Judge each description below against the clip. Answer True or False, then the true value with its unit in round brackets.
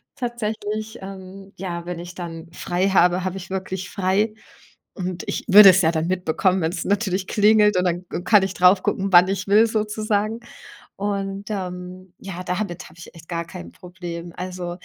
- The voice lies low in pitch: False (185 Hz)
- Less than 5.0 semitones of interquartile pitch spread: True (2.4 semitones)